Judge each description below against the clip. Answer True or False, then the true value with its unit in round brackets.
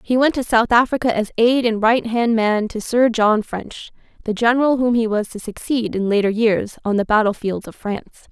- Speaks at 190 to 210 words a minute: True (200 wpm)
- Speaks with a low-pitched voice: False (225 Hz)